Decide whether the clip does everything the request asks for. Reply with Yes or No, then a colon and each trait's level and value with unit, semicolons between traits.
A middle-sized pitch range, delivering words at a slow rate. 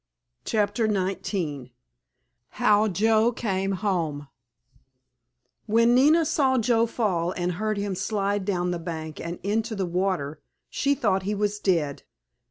Yes: average, 3.7 semitones; slow, 130 wpm